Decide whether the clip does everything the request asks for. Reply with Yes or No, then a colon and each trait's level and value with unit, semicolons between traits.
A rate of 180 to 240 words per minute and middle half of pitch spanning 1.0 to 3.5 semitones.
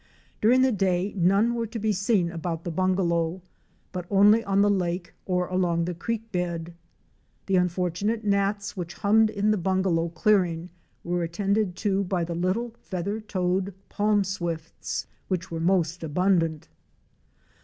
No: average, 150 wpm; average, 2.9 semitones